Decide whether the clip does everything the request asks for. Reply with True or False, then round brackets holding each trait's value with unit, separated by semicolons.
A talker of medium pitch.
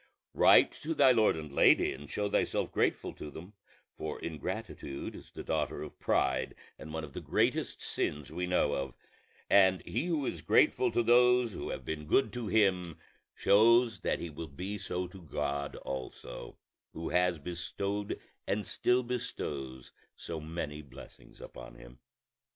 False (85 Hz)